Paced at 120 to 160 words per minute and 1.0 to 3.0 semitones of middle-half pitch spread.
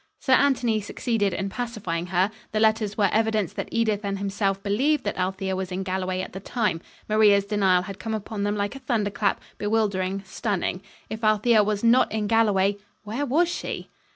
No: average, 180 wpm; narrow, 2.5 semitones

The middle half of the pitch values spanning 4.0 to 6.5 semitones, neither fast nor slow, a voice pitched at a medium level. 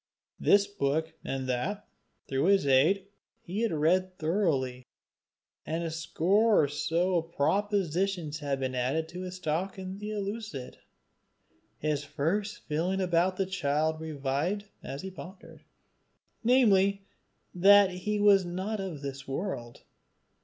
No: average, 5.0 semitones; slow, 130 wpm; medium, 175 Hz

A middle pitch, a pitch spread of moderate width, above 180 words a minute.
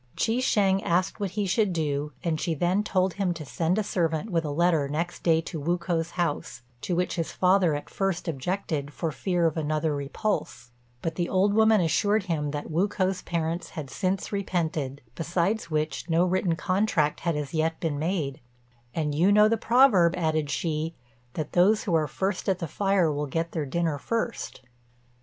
Yes: medium, 170 Hz; average, 3.4 semitones; average, 190 wpm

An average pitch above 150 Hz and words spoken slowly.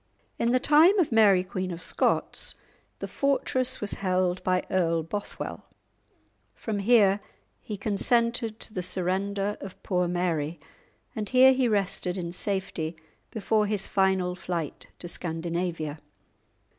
Yes: high, 190 Hz; slow, 130 wpm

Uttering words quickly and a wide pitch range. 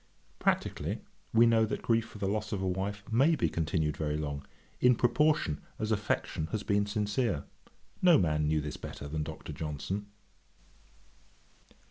No: average, 155 wpm; wide, 6.5 semitones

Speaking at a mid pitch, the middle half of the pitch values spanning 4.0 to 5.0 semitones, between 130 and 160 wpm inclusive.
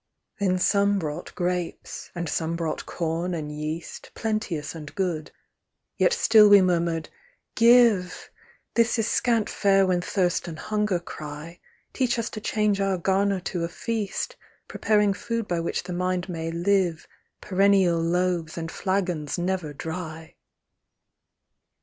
No: medium, 180 Hz; average, 3.3 semitones; average, 140 wpm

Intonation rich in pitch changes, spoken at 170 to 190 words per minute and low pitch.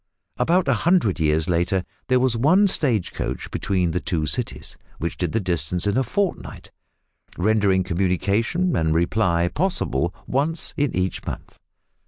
No: wide, 7.6 semitones; average, 150 wpm; low, 100 Hz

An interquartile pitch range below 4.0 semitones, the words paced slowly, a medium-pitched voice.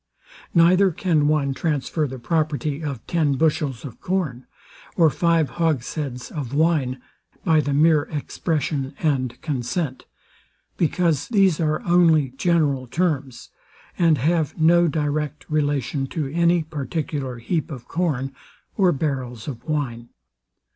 Yes: average, 3.4 semitones; slow, 125 wpm; medium, 150 Hz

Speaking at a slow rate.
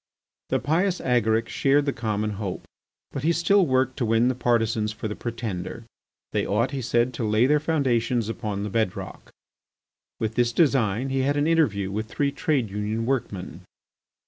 No: average, 170 wpm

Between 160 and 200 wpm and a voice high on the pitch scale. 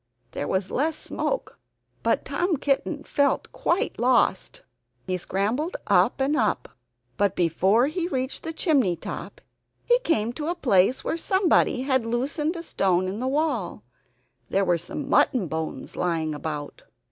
No: average, 150 wpm; very high, 250 Hz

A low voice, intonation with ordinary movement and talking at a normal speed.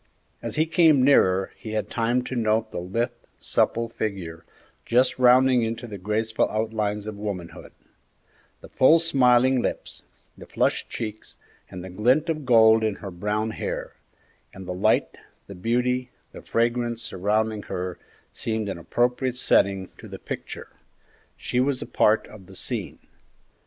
Yes: low, 110 Hz; average, 3.4 semitones; average, 150 wpm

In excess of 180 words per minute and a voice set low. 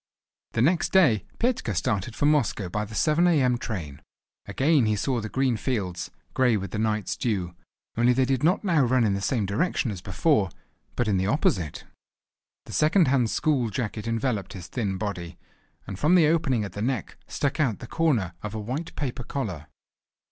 Yes: average, 190 wpm; low, 120 Hz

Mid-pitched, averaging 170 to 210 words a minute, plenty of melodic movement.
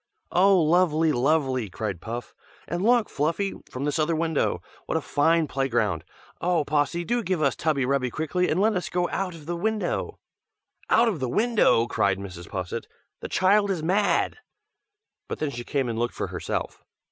Yes: medium, 155 Hz; average, 180 wpm; wide, 6.2 semitones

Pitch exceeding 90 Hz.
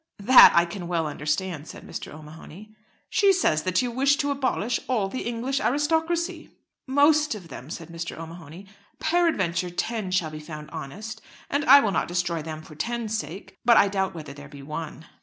Yes: high, 190 Hz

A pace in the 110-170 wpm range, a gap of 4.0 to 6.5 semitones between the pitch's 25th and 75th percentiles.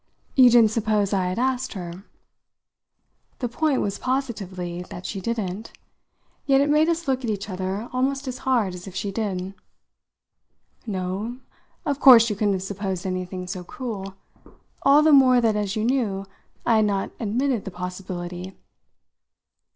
Yes: average, 160 wpm; average, 5.1 semitones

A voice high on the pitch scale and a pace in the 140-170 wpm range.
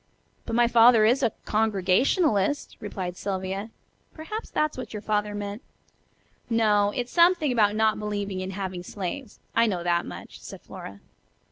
Yes: high, 210 Hz; average, 150 wpm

